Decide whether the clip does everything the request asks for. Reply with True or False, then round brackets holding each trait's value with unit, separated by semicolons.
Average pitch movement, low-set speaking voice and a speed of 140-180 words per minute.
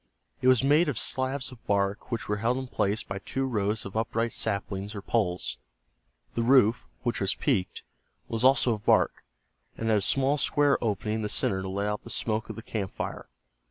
False (3.9 semitones; 110 Hz; 205 wpm)